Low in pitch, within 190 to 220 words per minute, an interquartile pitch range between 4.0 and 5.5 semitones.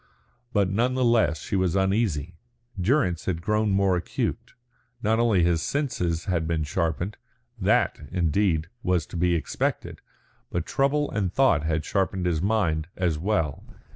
No: very low, 90 Hz; average, 150 wpm; average, 4.5 semitones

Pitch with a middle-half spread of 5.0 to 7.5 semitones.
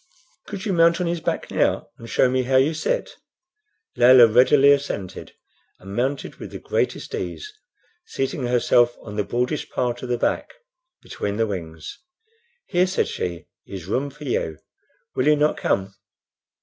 Yes: wide, 5.6 semitones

